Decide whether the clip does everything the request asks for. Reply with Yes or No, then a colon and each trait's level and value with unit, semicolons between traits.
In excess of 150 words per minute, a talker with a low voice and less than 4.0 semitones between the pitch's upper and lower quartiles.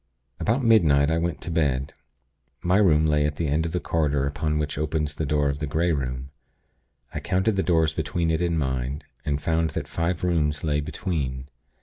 Yes: average, 200 wpm; very low, 75 Hz; narrow, 2.5 semitones